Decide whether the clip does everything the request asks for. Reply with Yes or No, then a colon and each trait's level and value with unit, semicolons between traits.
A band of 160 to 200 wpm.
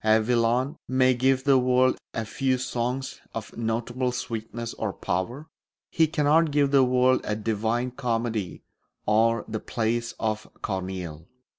No: average, 140 wpm